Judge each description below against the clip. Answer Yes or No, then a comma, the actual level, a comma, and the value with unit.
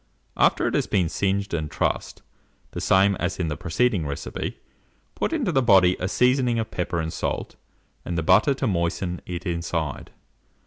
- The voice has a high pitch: No, very low, 90 Hz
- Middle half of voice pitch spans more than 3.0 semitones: Yes, average, 4.6 semitones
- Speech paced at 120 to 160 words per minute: No, average, 175 wpm